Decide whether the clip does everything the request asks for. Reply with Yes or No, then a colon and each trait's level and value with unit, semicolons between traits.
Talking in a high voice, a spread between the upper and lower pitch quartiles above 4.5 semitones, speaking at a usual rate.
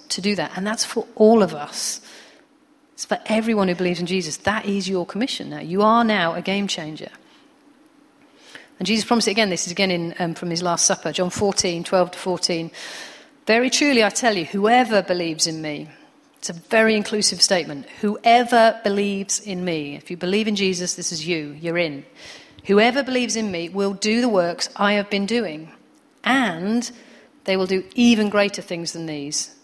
Yes: high, 205 Hz; average, 5.1 semitones; average, 190 wpm